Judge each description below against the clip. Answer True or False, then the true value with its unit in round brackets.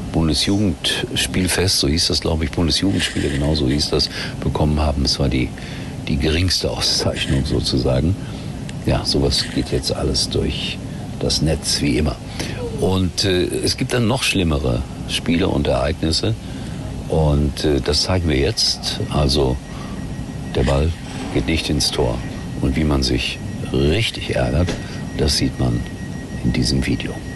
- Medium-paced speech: True (145 wpm)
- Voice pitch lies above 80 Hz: False (75 Hz)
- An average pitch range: True (5.0 semitones)